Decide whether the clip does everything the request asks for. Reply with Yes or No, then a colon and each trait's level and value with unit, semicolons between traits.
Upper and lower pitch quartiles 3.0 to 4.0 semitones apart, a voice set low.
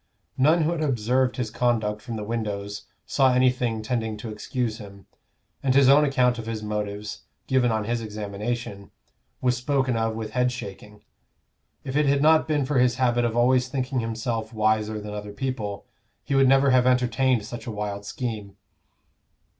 Yes: average, 3.4 semitones; low, 120 Hz